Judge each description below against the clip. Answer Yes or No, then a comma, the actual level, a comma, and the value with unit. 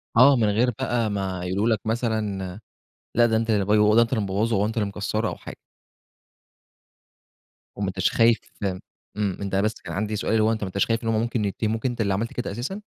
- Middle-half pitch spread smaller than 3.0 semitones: Yes, narrow, 2.4 semitones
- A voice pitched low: Yes, low, 110 Hz